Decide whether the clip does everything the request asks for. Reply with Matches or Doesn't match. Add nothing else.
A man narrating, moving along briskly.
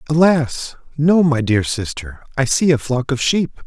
Doesn't match